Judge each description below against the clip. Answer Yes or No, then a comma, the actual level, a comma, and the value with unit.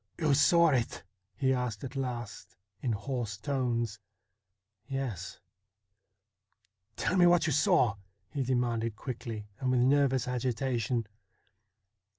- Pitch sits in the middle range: No, low, 125 Hz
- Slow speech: Yes, slow, 130 wpm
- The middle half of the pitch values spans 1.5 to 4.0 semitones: Yes, average, 3.1 semitones